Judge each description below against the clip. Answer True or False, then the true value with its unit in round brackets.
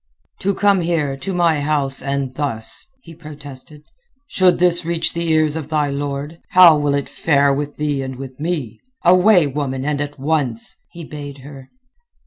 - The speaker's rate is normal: True (170 wpm)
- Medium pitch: True (145 Hz)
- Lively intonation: False (3.1 semitones)